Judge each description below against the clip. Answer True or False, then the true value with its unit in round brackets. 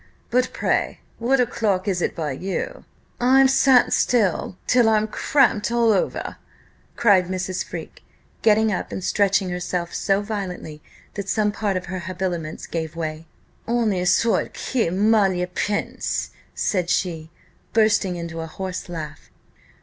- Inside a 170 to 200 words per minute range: False (140 wpm)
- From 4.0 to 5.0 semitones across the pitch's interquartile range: False (3.6 semitones)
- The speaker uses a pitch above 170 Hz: True (190 Hz)